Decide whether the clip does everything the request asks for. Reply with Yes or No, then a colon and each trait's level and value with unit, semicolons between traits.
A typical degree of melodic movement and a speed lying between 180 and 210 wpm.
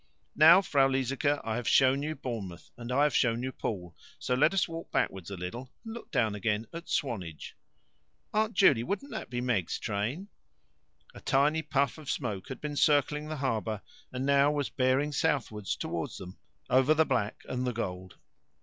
Yes: average, 4.9 semitones; average, 185 wpm